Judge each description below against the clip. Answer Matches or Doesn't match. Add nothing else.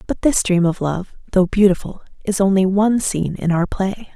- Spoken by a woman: Matches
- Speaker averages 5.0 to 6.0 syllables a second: Matches